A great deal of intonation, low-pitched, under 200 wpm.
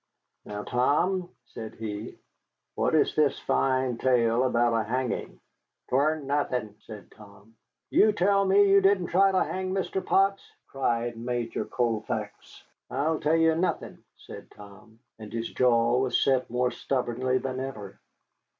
Yes: wide, 6.0 semitones; low, 130 Hz; average, 140 wpm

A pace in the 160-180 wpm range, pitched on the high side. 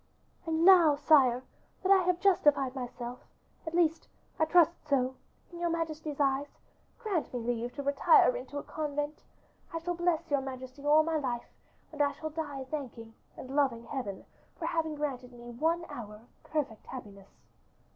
Yes: average, 165 wpm; very high, 290 Hz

